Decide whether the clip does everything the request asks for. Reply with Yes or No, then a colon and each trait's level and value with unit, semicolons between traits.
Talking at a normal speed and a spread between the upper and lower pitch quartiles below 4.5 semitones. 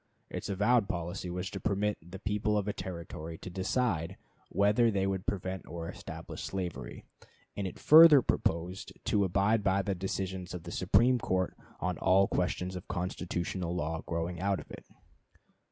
Yes: average, 165 wpm; narrow, 2.4 semitones